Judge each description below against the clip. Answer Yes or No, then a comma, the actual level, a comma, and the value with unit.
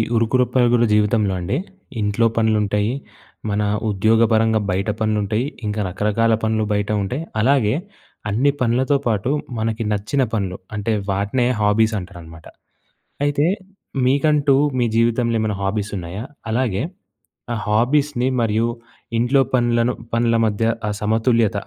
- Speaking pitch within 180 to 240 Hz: No, low, 110 Hz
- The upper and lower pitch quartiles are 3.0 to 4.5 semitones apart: No, narrow, 2.5 semitones